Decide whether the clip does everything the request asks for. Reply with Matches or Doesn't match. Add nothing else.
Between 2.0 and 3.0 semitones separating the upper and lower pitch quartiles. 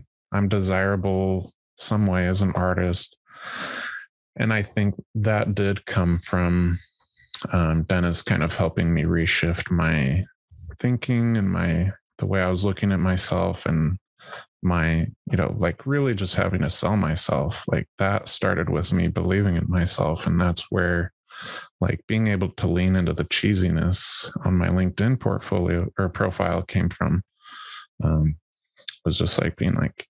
Matches